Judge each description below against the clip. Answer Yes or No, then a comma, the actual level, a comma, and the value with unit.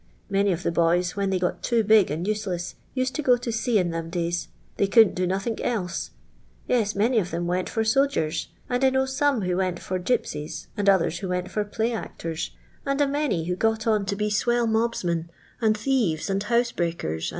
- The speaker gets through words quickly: Yes, fast, 215 wpm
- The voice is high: Yes, high, 200 Hz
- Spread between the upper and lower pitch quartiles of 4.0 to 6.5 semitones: Yes, average, 4.8 semitones